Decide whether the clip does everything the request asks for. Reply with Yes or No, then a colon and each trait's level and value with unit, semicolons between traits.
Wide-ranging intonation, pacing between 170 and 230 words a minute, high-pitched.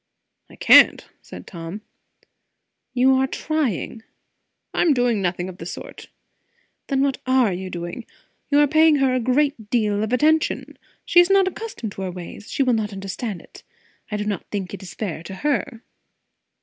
Yes: wide, 6.2 semitones; average, 175 wpm; high, 230 Hz